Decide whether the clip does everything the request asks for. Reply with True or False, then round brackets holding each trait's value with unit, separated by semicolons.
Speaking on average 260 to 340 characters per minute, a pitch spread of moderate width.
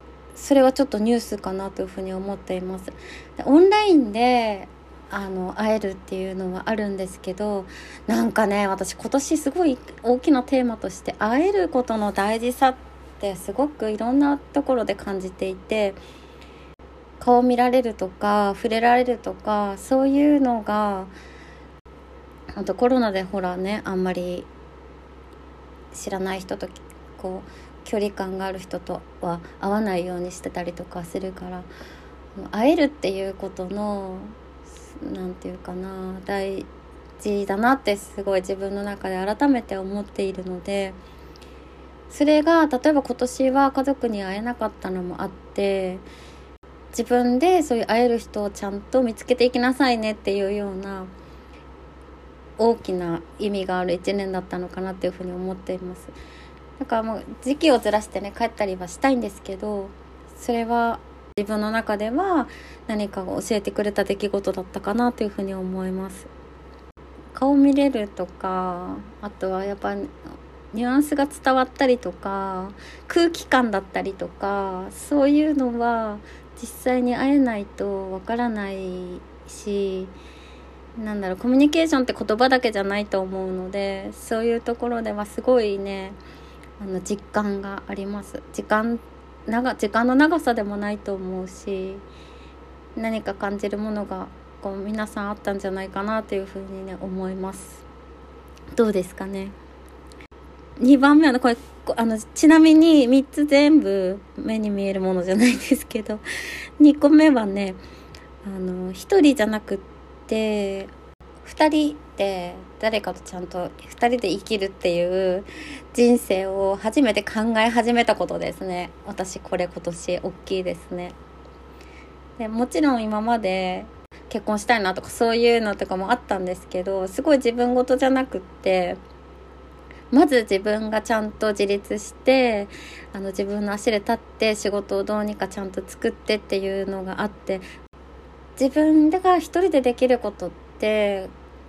True (300 characters per minute; 4.2 semitones)